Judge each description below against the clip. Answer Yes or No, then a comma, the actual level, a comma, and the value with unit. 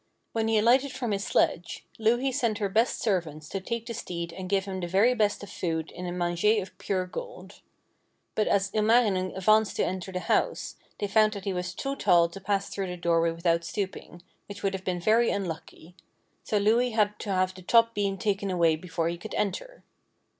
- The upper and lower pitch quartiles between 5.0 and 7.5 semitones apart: No, average, 3.4 semitones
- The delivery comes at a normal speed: No, fast, 210 wpm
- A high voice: Yes, high, 195 Hz